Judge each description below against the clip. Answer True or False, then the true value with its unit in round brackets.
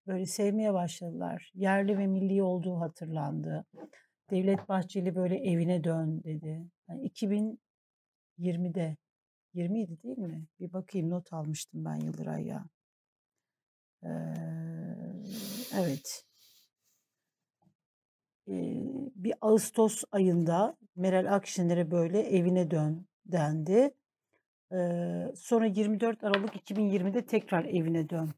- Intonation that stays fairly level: False (3.7 semitones)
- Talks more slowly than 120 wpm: True (100 wpm)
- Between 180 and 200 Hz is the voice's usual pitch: True (185 Hz)